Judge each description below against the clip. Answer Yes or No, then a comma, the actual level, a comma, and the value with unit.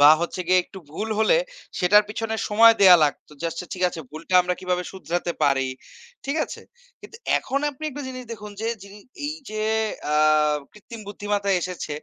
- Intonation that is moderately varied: Yes, average, 4.0 semitones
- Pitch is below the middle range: No, high, 200 Hz